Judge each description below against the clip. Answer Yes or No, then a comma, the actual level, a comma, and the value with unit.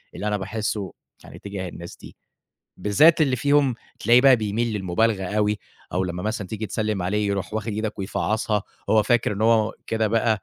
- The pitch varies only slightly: Yes, narrow, 2.1 semitones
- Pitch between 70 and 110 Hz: Yes, low, 105 Hz